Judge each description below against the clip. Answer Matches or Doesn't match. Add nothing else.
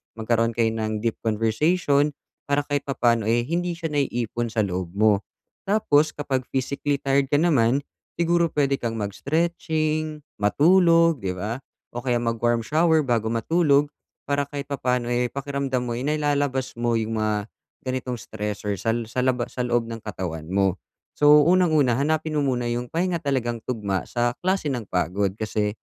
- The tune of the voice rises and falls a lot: Doesn't match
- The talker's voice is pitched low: Matches